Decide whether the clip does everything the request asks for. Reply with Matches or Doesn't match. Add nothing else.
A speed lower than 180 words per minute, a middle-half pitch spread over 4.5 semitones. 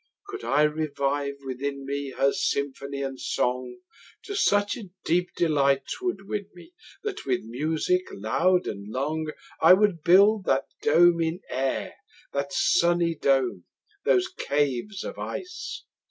Matches